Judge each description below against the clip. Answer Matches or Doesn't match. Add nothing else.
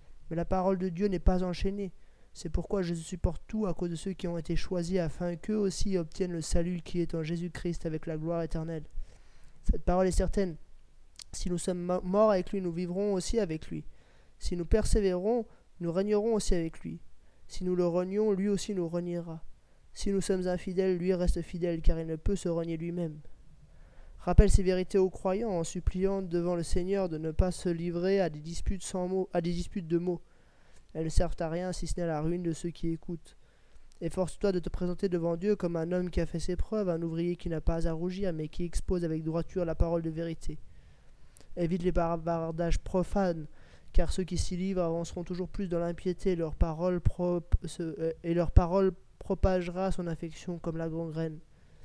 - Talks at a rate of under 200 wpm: Doesn't match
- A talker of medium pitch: Matches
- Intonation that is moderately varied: Doesn't match